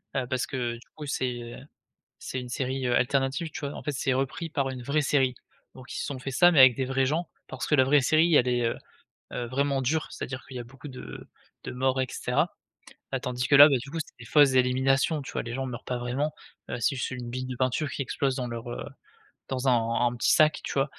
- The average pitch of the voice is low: Yes, low, 130 Hz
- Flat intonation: Yes, narrow, 2.1 semitones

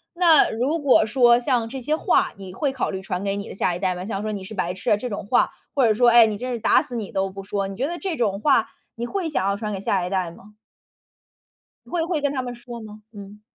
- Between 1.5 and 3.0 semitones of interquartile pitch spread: No, average, 4.5 semitones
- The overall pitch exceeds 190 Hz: Yes, high, 220 Hz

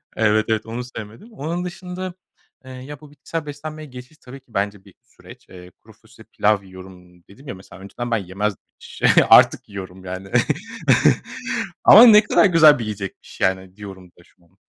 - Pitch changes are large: Yes, wide, 7.4 semitones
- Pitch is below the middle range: Yes, low, 110 Hz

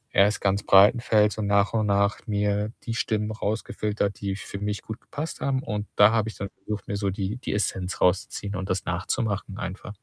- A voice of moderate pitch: No, low, 105 Hz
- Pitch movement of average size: No, narrow, 1.5 semitones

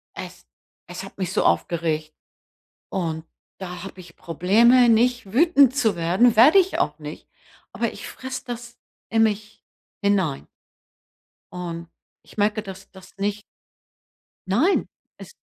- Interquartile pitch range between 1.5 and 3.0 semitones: No, average, 5.0 semitones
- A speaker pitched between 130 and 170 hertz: No, high, 200 Hz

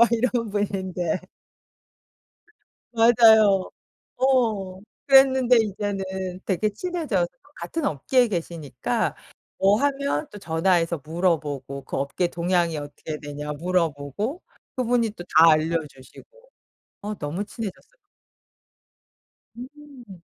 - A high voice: Yes, high, 195 Hz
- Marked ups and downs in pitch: Yes, wide, 6.5 semitones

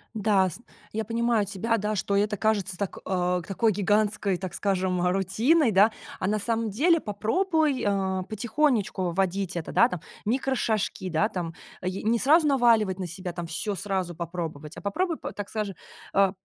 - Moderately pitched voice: No, high, 200 Hz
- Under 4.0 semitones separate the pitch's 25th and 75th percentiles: Yes, average, 3.5 semitones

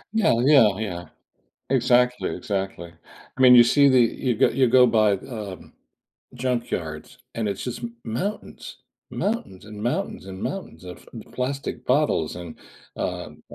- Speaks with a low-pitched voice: Yes, low, 120 Hz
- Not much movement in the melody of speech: No, average, 4.6 semitones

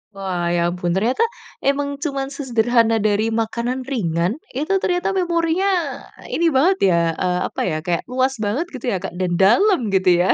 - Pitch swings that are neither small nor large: No, wide, 6.9 semitones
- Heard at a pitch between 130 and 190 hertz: No, high, 240 Hz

